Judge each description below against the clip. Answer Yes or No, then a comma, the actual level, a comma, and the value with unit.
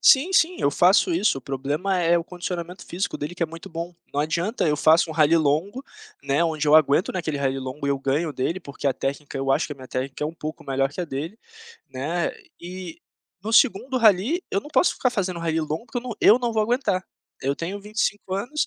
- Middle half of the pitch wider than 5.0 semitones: Yes, wide, 5.5 semitones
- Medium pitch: Yes, medium, 170 Hz